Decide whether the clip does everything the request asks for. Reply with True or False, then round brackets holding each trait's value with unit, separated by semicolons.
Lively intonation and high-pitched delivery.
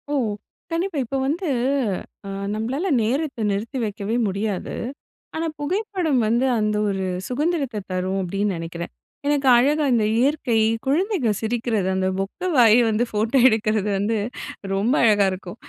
True (5.9 semitones; 225 Hz)